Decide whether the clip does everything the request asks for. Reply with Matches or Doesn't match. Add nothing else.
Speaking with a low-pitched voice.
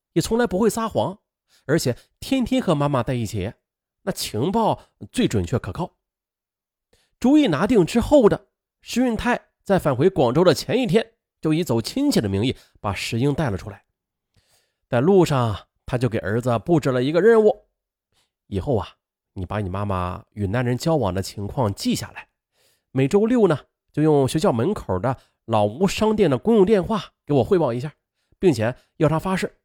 Doesn't match